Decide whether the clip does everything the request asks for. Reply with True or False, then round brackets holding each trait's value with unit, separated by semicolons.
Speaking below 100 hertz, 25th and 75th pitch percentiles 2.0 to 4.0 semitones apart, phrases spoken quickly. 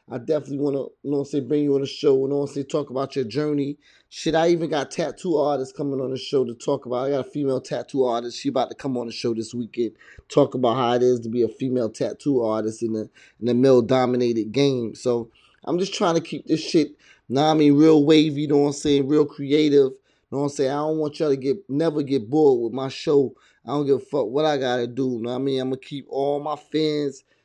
False (140 Hz; 2.9 semitones; 270 wpm)